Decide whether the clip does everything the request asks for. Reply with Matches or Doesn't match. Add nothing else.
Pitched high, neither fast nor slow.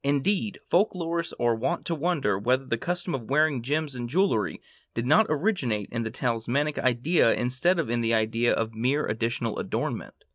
Doesn't match